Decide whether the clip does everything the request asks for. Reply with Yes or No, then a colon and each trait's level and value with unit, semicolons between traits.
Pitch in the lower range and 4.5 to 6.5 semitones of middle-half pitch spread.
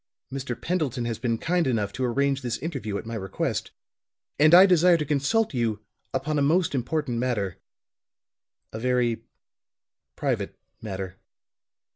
Yes: low, 125 Hz; average, 5.1 semitones